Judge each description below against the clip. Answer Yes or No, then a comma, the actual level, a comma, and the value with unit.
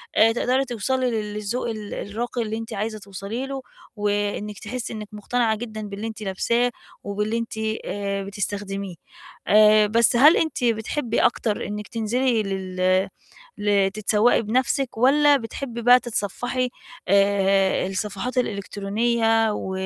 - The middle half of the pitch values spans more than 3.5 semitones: No, average, 3.0 semitones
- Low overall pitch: No, high, 215 Hz